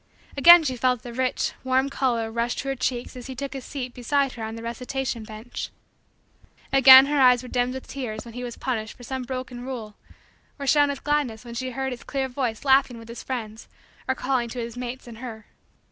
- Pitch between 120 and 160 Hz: No, very high, 250 Hz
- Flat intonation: Yes, narrow, 2.2 semitones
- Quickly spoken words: Yes, fast, 220 wpm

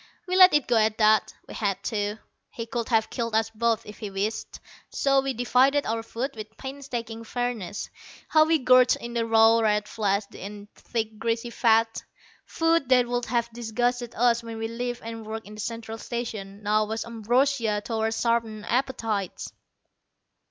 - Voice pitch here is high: Yes, high, 230 Hz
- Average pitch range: No, narrow, 2.1 semitones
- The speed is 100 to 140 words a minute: No, average, 175 wpm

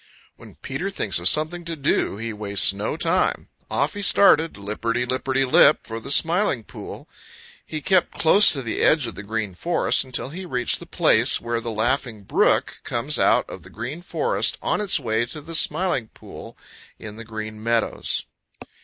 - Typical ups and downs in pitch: No, wide, 6.7 semitones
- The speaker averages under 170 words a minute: No, average, 180 wpm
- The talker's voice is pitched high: No, low, 130 Hz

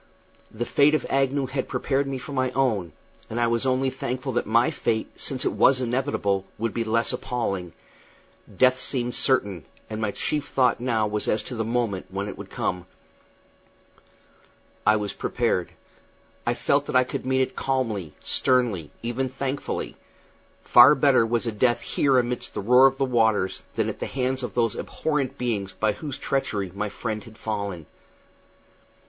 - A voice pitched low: Yes, low, 120 Hz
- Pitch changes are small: No, average, 3.4 semitones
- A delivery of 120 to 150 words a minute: No, average, 170 wpm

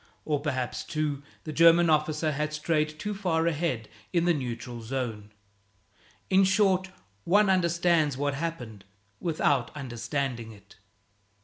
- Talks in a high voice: No, medium, 155 Hz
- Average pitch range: Yes, average, 4.8 semitones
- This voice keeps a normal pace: No, slow, 125 wpm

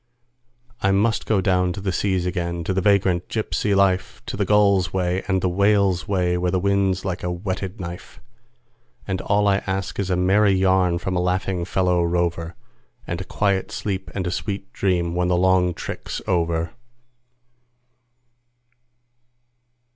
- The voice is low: Yes, very low, 95 Hz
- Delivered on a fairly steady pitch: Yes, narrow, 1.7 semitones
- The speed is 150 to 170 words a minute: Yes, average, 160 wpm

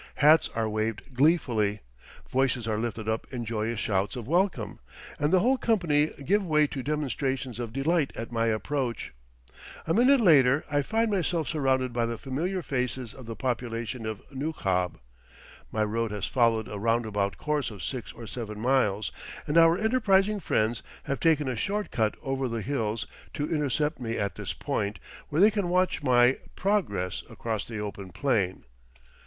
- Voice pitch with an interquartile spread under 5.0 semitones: No, wide, 5.5 semitones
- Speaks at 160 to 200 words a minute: Yes, average, 170 wpm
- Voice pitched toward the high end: No, low, 130 Hz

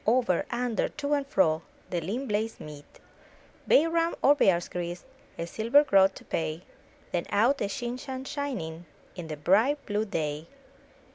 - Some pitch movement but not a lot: No, wide, 7.6 semitones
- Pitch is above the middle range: Yes, high, 210 Hz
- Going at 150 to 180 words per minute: Yes, average, 165 wpm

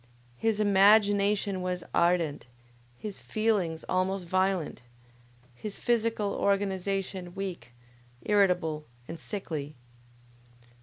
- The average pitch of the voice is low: No, high, 195 Hz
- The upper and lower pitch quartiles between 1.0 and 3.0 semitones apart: Yes, narrow, 2.5 semitones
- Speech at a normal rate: No, slow, 85 wpm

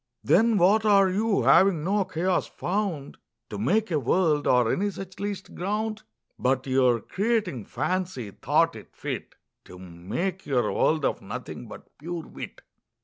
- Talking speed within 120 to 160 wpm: Yes, average, 150 wpm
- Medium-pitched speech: Yes, medium, 180 Hz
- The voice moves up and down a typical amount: No, wide, 7.1 semitones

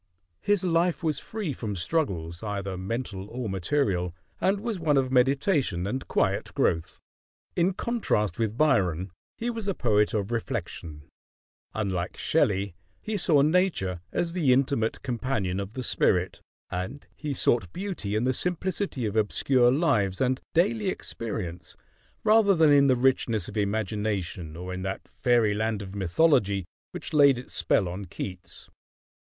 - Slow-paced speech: No, average, 150 wpm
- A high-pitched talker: No, low, 115 Hz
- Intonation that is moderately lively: No, wide, 7.8 semitones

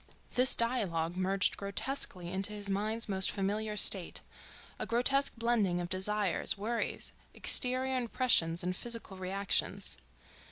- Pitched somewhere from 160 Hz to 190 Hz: No, high, 205 Hz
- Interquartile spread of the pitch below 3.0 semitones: No, average, 3.9 semitones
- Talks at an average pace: No, slow, 115 wpm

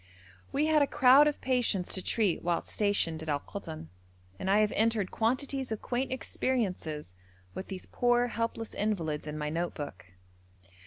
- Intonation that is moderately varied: No, wide, 6.8 semitones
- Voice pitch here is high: Yes, high, 210 Hz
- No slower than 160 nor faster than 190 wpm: Yes, average, 165 wpm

